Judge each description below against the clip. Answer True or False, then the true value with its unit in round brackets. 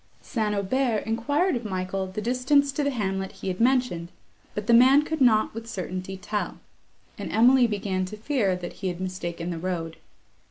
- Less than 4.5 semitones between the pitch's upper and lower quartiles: False (5.1 semitones)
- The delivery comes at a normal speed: True (185 wpm)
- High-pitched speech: True (210 Hz)